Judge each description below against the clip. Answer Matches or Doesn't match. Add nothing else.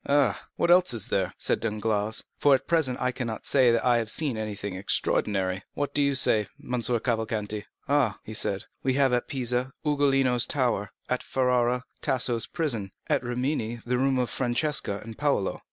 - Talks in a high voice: Doesn't match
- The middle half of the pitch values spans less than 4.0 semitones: Matches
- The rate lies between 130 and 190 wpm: Matches